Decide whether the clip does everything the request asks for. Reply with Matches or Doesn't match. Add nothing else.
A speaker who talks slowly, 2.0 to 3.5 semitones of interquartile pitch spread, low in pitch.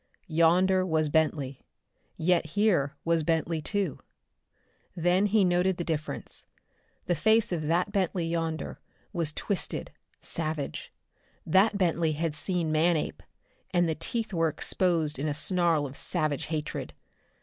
Doesn't match